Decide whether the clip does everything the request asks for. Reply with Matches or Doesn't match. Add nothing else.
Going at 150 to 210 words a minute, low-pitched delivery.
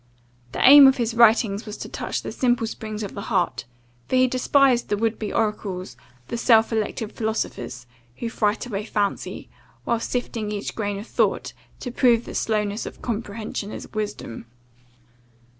Doesn't match